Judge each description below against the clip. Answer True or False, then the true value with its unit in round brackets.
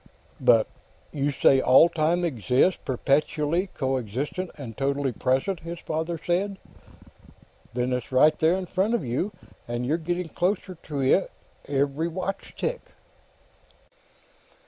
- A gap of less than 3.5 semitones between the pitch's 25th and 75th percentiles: False (5.0 semitones)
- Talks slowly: True (125 wpm)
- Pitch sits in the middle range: True (155 Hz)